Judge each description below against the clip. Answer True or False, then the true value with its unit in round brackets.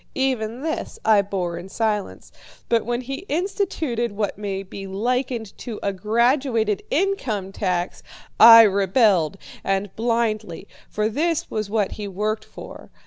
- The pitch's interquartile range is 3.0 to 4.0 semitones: True (3.5 semitones)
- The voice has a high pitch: True (215 Hz)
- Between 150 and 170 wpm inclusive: False (140 wpm)